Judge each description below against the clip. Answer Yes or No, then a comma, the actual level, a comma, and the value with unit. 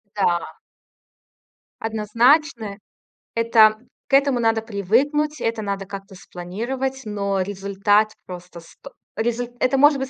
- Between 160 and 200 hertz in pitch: No, high, 220 Hz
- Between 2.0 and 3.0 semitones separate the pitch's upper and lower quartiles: No, average, 4.3 semitones